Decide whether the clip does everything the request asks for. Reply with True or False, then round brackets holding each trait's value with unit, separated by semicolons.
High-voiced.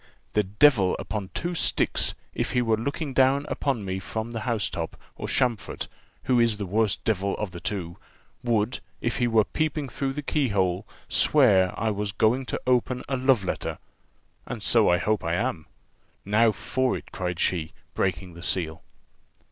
False (110 Hz)